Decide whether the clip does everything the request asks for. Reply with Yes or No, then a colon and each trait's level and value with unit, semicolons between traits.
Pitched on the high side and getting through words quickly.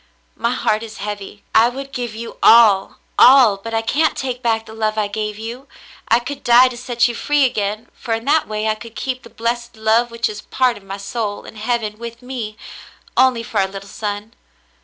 Yes: high, 230 Hz; fast, 215 wpm